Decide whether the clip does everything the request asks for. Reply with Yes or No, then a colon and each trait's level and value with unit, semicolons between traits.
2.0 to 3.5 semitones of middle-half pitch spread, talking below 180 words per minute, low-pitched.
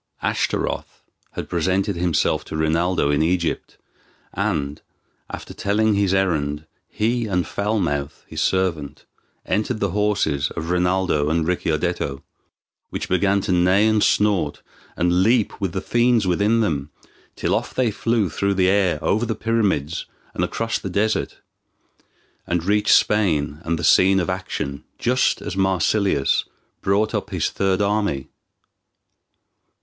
No: average, 4.1 semitones; average, 140 wpm; very low, 95 Hz